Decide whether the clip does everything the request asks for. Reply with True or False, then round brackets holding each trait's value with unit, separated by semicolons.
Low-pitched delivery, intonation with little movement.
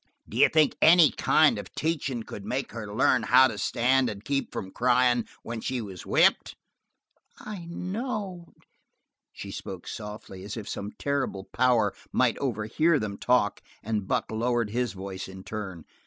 False (120 Hz; 4.8 semitones)